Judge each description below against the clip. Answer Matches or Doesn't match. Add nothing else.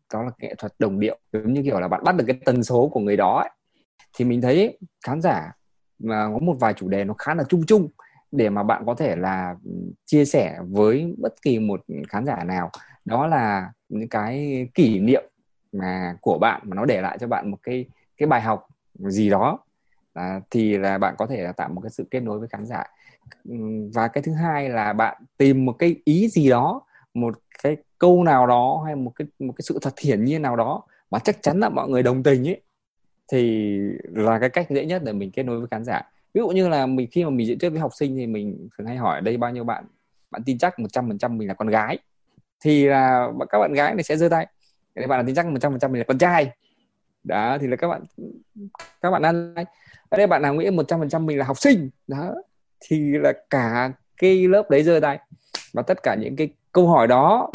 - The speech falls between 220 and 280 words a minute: Matches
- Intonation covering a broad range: Matches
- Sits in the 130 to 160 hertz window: Matches